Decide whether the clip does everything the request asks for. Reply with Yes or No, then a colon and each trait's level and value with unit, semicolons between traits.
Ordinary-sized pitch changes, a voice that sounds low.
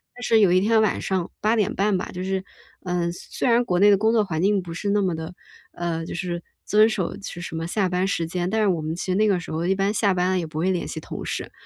No: average, 3.1 semitones; medium, 185 Hz